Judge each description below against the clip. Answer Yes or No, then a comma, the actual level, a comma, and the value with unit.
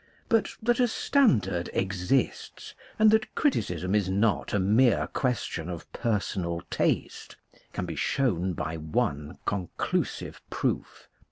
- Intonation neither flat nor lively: No, wide, 7.5 semitones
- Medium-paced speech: No, slow, 120 wpm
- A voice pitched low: Yes, low, 100 Hz